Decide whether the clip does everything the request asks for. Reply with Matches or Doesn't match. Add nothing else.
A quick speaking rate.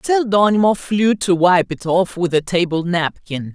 Doesn't match